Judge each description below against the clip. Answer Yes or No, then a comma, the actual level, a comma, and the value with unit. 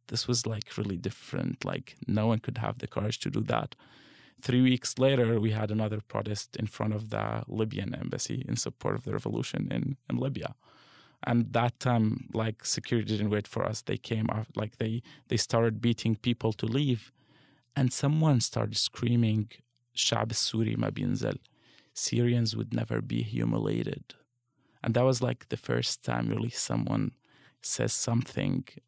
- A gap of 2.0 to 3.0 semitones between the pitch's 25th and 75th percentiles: Yes, narrow, 2.6 semitones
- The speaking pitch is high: No, low, 120 Hz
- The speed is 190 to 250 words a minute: No, average, 165 wpm